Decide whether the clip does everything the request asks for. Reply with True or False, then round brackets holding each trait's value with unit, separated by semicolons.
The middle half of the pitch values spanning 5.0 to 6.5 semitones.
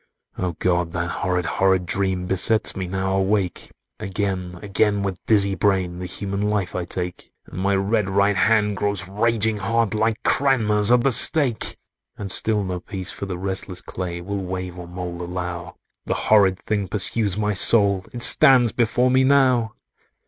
False (2.8 semitones)